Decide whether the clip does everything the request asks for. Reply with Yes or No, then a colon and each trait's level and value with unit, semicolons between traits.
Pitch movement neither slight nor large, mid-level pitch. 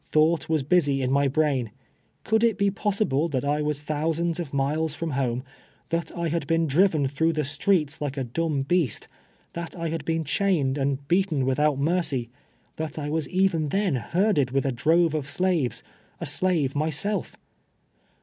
Yes: average, 3.5 semitones; medium, 155 Hz